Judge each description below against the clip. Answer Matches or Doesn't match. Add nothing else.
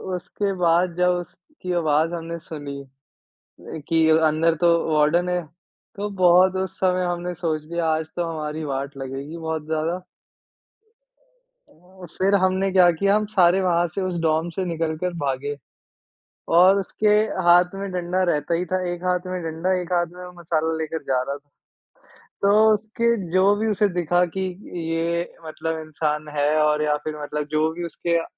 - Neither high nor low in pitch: Matches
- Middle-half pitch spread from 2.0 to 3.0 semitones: Matches